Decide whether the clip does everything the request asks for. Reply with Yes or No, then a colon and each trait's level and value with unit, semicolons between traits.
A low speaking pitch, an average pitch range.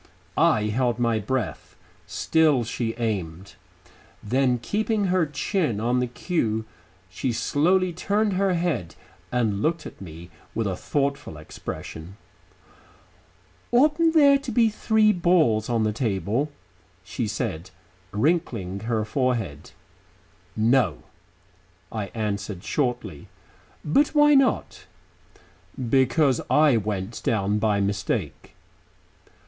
No: low, 120 Hz; wide, 8.0 semitones